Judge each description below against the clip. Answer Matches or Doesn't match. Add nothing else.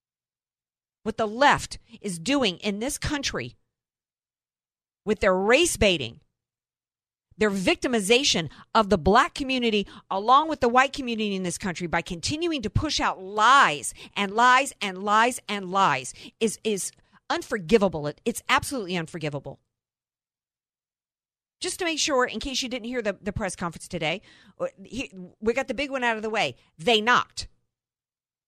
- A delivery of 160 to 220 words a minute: Doesn't match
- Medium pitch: Doesn't match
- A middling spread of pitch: Doesn't match